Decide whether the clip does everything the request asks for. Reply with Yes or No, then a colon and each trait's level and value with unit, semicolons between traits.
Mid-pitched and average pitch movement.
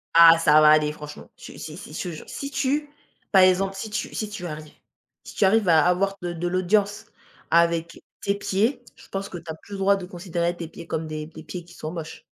Yes: medium, 175 Hz; average, 3.5 semitones